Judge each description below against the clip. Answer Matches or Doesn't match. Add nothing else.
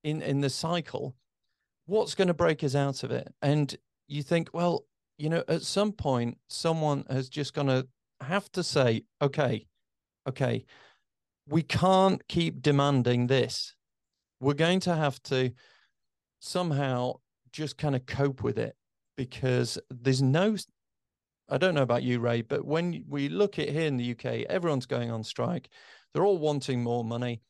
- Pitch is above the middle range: Doesn't match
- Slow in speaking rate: Doesn't match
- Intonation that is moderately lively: Matches